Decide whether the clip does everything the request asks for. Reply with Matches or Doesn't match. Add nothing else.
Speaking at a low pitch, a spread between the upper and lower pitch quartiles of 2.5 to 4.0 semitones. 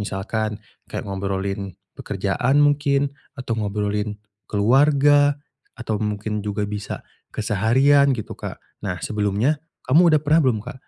Doesn't match